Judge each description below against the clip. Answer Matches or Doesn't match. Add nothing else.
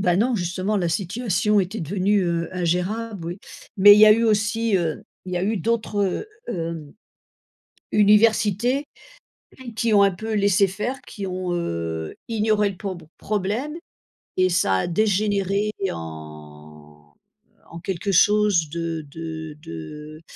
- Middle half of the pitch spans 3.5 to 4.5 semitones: Matches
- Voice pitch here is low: Doesn't match